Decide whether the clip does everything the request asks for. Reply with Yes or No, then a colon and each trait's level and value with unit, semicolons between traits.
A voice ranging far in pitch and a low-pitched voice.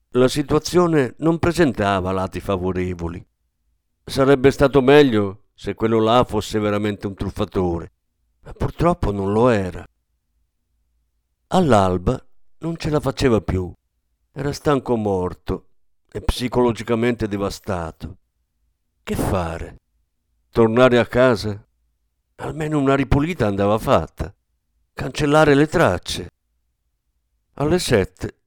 Yes: wide, 8.7 semitones; low, 100 Hz